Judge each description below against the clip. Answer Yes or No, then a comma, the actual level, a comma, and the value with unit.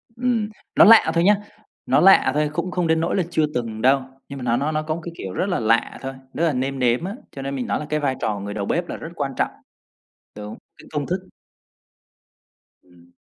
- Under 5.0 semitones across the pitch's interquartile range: No, wide, 5.5 semitones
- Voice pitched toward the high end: No, medium, 145 Hz